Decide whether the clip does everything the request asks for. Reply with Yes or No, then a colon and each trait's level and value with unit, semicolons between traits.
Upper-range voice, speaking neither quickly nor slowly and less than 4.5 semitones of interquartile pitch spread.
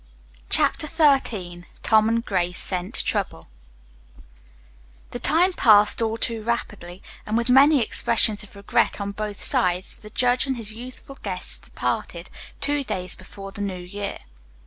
Yes: high, 215 Hz; average, 145 wpm; average, 4.0 semitones